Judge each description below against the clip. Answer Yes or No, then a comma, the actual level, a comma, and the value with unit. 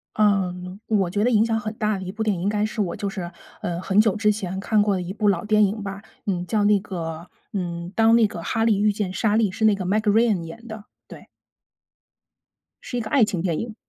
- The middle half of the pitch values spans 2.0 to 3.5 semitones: Yes, narrow, 2.6 semitones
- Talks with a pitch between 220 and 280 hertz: No, high, 205 Hz